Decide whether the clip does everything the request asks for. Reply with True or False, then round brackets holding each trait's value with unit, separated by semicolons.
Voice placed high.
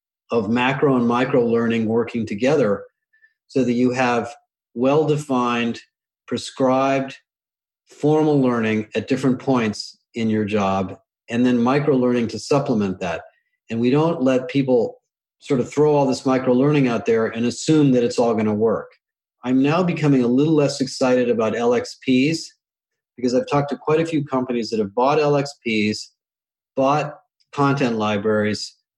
False (130 Hz)